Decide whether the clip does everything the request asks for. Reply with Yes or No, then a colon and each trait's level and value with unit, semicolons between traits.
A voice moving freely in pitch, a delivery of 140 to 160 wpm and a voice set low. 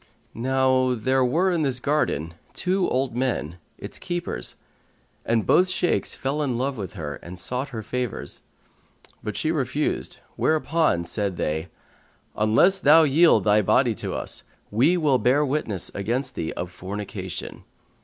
Yes: wide, 6.5 semitones; average, 145 wpm; low, 130 Hz